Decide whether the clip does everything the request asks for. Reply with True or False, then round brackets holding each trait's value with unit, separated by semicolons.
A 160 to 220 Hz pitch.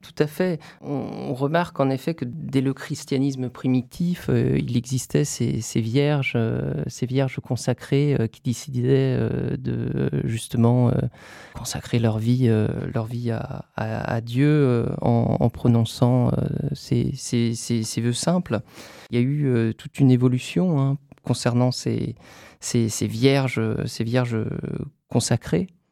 False (125 Hz)